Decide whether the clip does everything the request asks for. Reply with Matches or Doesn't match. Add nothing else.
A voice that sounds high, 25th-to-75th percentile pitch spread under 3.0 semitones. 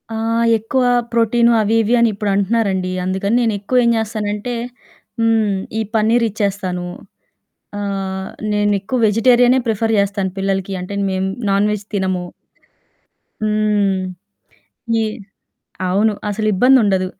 Matches